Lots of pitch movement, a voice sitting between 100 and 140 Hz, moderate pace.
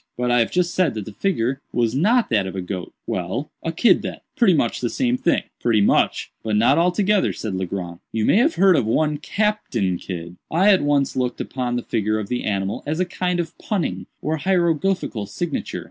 No: wide, 8.9 semitones; low, 135 Hz; fast, 210 wpm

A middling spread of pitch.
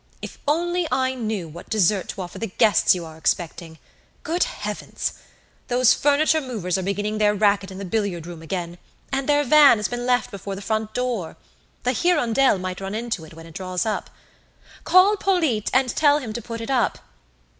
No: wide, 5.9 semitones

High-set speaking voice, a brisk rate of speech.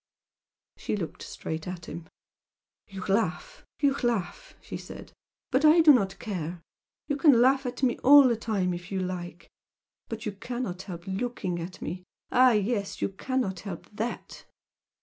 No: high, 205 Hz; average, 160 wpm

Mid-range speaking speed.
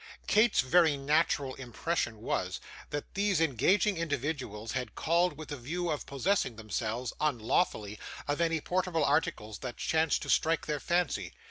Yes: average, 145 wpm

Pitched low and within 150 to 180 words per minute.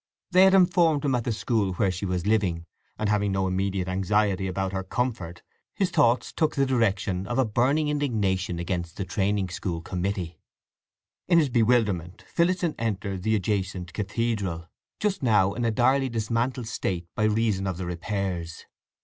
Yes: low, 105 Hz; average, 165 wpm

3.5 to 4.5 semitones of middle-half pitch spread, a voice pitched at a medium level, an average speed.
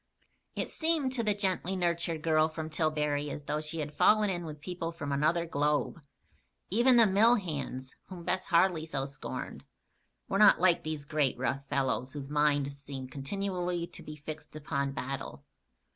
Yes: average, 4.1 semitones; medium, 155 Hz; average, 170 wpm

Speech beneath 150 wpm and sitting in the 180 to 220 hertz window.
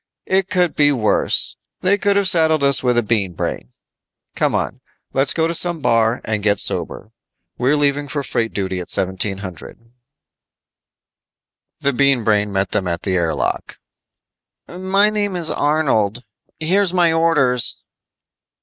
No: average, 140 wpm; medium, 140 Hz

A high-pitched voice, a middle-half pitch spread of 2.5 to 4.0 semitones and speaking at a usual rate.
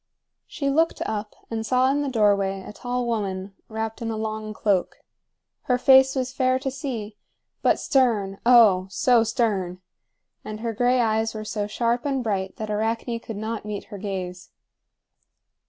Yes: high, 225 Hz; average, 3.2 semitones; average, 165 wpm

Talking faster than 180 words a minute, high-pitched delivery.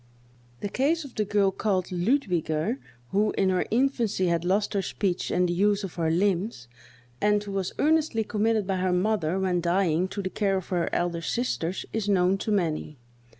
Yes: average, 190 wpm; high, 195 Hz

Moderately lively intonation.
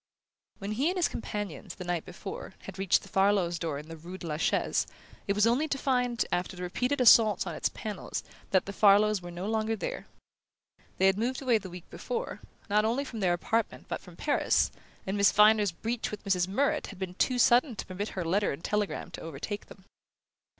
Yes: average, 3.9 semitones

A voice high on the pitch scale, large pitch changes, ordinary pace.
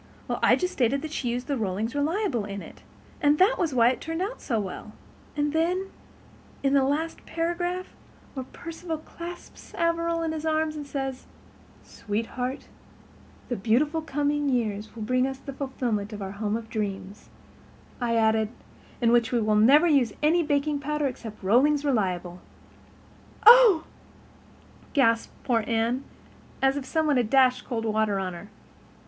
Yes: very high, 265 Hz; wide, 5.7 semitones; average, 165 wpm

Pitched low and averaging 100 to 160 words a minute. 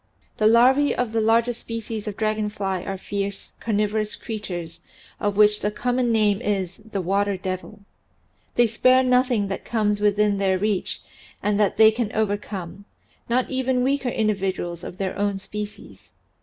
No: high, 210 Hz; average, 155 wpm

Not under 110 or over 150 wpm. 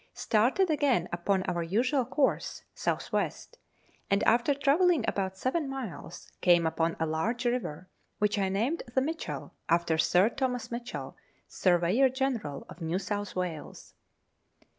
Yes: average, 140 wpm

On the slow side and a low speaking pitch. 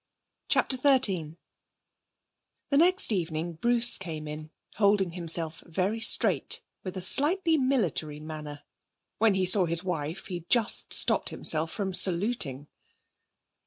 No: slow, 125 wpm; medium, 185 Hz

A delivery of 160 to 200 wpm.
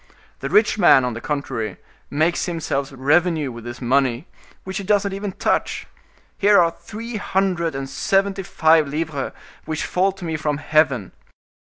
Yes: average, 165 wpm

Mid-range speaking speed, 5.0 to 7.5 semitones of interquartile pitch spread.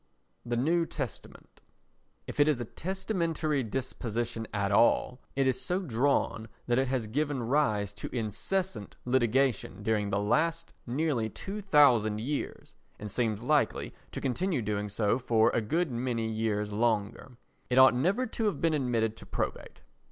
Yes: average, 155 wpm; average, 5.3 semitones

